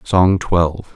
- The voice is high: No, very low, 90 Hz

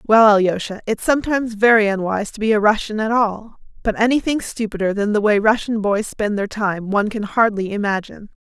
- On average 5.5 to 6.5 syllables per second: Yes, 5.7 syllables/s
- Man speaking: No, female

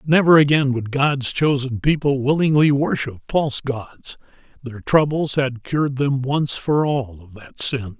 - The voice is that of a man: Yes, male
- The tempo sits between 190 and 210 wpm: No, average, 160 wpm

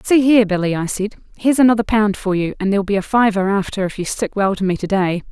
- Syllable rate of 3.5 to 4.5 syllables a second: No, 6.5 syllables/s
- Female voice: Yes, female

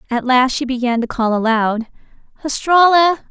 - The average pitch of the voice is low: No, very high, 260 Hz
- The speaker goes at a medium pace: Yes, average, 145 wpm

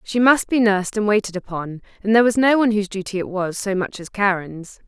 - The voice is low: No, high, 205 Hz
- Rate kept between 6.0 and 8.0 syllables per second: Yes, 6.2 syllables/s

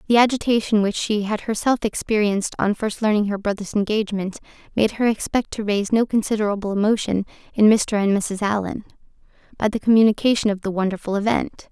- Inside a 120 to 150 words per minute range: No, average, 170 wpm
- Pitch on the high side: Yes, high, 210 Hz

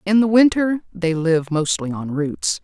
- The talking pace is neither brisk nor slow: Yes, average, 185 wpm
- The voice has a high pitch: No, medium, 175 Hz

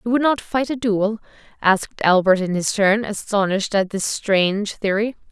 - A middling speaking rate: Yes, average, 180 wpm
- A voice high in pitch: Yes, high, 210 Hz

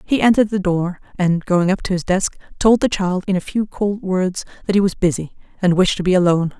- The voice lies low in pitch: No, high, 190 Hz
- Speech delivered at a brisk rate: Yes, fast, 245 wpm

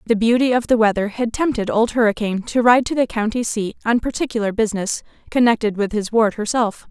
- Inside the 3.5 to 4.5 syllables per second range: No, 6.0 syllables/s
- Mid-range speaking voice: No, high, 225 Hz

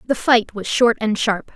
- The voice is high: Yes, high, 225 Hz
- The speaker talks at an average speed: No, fast, 230 wpm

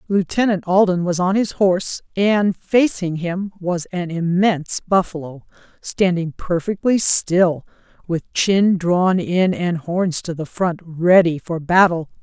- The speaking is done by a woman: Yes, female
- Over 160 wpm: No, slow, 135 wpm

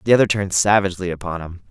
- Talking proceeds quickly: Yes, fast, 210 wpm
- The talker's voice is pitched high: No, very low, 95 Hz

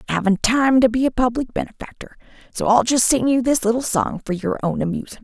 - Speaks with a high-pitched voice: Yes, high, 235 Hz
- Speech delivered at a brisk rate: Yes, fast, 220 wpm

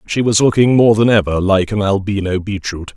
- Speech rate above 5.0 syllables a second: Yes, 5.3 syllables/s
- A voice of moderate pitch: No, low, 100 Hz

